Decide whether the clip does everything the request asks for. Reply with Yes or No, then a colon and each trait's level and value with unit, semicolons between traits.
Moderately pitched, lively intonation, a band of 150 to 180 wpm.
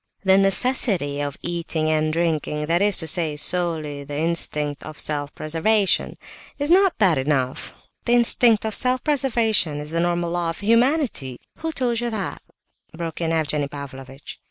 Yes: medium, 170 Hz; wide, 6.6 semitones; average, 160 wpm